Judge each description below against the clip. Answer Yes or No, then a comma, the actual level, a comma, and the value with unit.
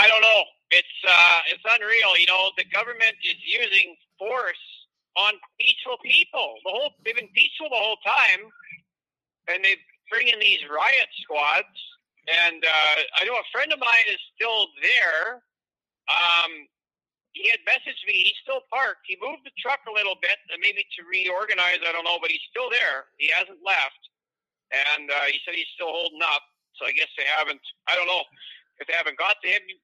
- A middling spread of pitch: No, wide, 8.4 semitones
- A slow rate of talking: No, average, 185 wpm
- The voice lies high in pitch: Yes, high, 200 Hz